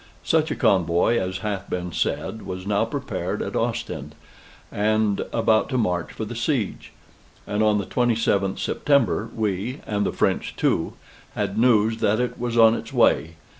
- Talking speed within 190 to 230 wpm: No, average, 165 wpm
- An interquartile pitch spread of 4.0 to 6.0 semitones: No, average, 2.7 semitones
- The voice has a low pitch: Yes, low, 110 Hz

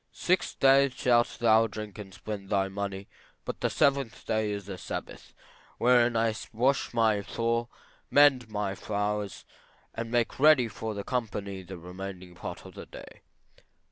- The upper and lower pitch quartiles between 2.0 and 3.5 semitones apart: Yes, average, 3.2 semitones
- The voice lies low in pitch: Yes, low, 110 Hz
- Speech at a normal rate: Yes, average, 160 wpm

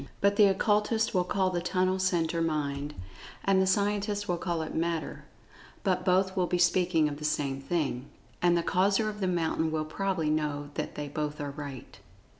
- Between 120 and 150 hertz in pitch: No, medium, 175 Hz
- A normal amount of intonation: Yes, average, 3.8 semitones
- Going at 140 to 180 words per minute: No, average, 190 wpm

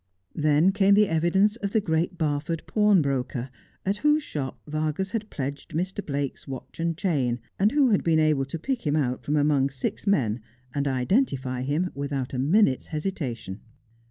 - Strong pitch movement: Yes, wide, 6.0 semitones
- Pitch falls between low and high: Yes, medium, 155 Hz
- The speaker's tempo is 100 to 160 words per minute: No, average, 170 wpm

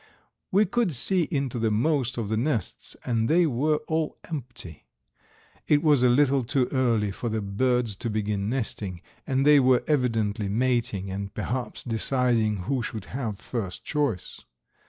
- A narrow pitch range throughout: No, average, 4.4 semitones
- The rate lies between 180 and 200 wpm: No, average, 155 wpm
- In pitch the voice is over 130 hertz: No, low, 120 Hz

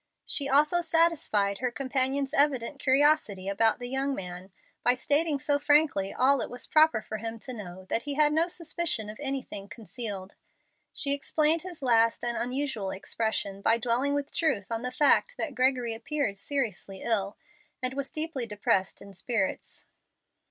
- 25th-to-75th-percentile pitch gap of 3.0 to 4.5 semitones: No, average, 5.1 semitones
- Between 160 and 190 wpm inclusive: Yes, average, 165 wpm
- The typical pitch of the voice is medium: No, very high, 255 Hz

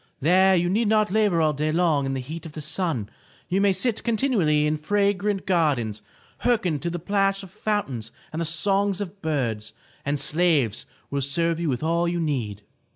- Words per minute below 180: No, average, 195 wpm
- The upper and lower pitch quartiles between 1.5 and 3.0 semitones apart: No, average, 4.9 semitones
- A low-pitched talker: No, medium, 170 Hz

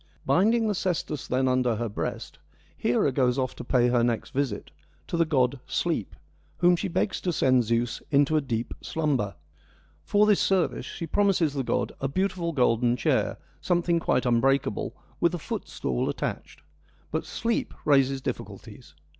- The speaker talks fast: No, average, 165 wpm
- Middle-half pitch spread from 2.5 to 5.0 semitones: No, wide, 5.6 semitones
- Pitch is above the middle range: No, low, 135 Hz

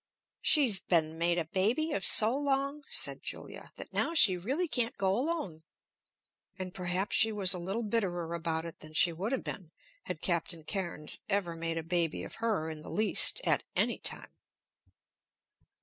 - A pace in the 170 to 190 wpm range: Yes, average, 175 wpm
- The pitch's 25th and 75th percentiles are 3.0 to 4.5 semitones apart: No, wide, 5.4 semitones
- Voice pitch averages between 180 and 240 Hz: Yes, medium, 185 Hz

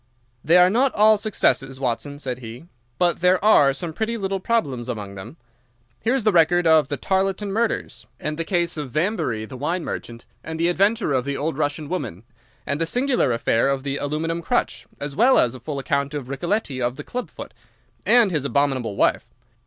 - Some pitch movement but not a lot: No, wide, 6.0 semitones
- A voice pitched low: No, medium, 155 Hz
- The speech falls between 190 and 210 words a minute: Yes, average, 195 wpm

